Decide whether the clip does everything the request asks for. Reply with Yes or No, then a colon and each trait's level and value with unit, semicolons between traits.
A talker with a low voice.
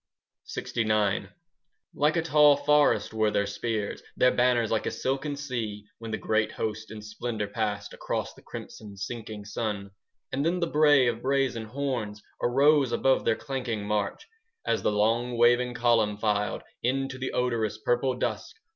Yes: low, 115 Hz